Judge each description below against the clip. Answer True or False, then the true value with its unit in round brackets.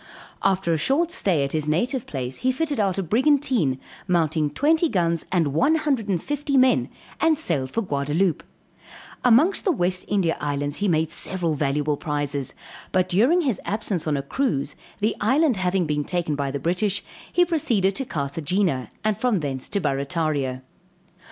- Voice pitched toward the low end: False (180 Hz)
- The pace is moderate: True (170 wpm)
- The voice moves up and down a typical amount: False (8.6 semitones)